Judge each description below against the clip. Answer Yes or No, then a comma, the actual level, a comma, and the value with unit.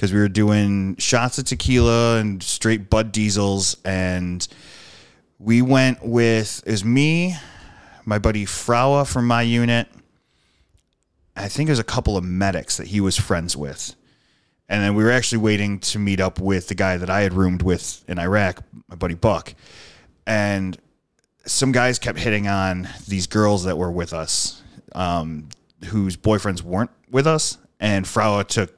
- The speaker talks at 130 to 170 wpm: Yes, average, 165 wpm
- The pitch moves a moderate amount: Yes, average, 3.9 semitones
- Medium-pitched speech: No, low, 100 Hz